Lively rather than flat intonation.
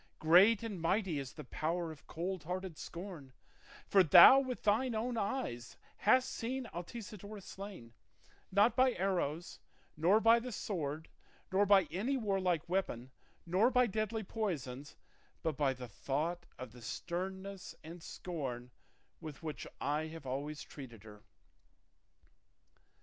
Yes: wide, 5.7 semitones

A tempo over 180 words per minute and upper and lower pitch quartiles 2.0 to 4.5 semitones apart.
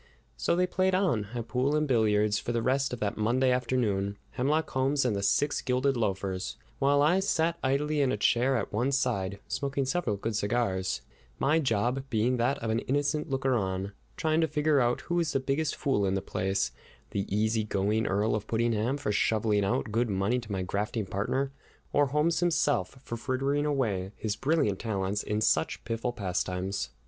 No: average, 190 wpm; average, 5.1 semitones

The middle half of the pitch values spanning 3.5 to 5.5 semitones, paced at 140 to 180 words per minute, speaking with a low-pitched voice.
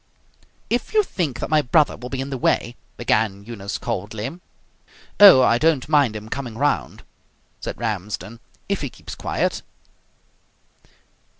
Yes: average, 5.0 semitones; average, 145 wpm; low, 125 Hz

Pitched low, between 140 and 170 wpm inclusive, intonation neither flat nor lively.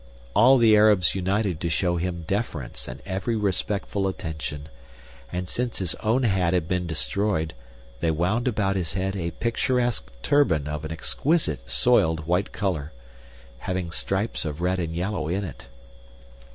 Yes: very low, 90 Hz; average, 150 wpm; average, 4.5 semitones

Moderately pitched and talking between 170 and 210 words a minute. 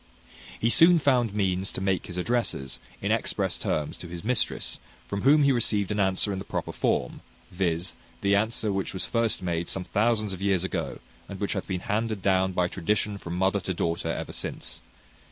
No: low, 100 Hz; average, 195 wpm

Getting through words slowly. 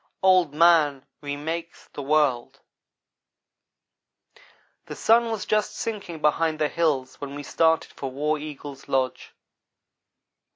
Yes: slow, 115 wpm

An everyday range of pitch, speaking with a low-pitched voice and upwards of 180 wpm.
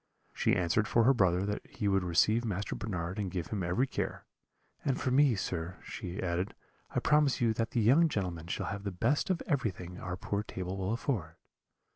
Yes: average, 4.7 semitones; low, 100 Hz; average, 200 wpm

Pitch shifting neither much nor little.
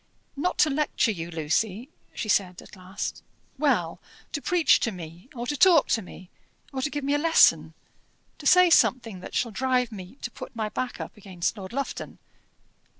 No: wide, 7.1 semitones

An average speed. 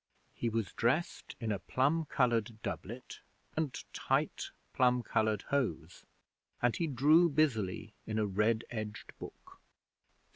No: slow, 130 wpm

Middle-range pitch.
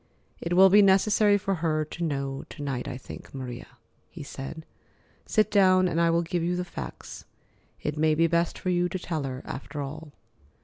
Yes: medium, 165 Hz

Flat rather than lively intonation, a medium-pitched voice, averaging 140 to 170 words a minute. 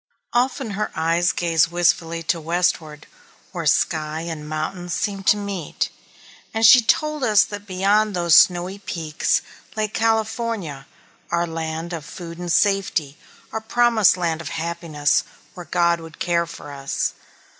No: average, 4.0 semitones; medium, 175 Hz; average, 145 wpm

